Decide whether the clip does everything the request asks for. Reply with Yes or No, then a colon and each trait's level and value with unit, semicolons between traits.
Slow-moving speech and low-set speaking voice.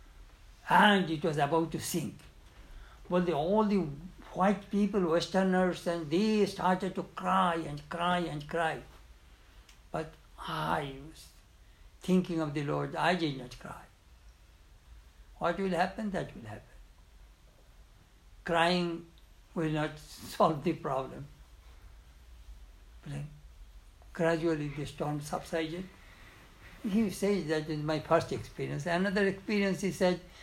No: slow, 120 wpm; medium, 155 Hz